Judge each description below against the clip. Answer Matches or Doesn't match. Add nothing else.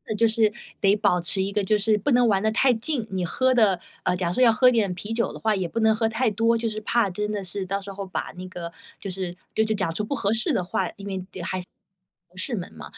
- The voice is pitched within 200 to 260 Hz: Matches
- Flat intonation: Doesn't match